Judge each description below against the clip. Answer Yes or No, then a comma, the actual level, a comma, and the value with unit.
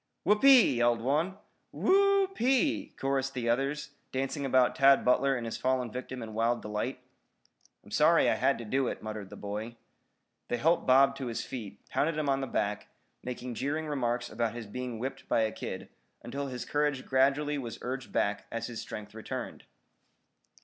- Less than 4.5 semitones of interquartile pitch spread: Yes, average, 3.2 semitones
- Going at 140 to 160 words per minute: No, average, 190 wpm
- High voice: No, low, 130 Hz